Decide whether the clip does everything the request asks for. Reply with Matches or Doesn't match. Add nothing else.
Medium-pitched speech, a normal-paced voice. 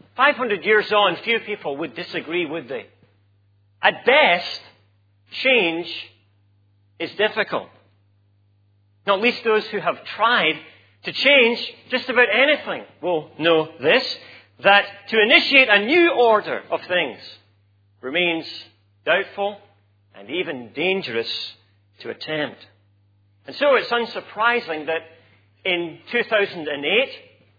Doesn't match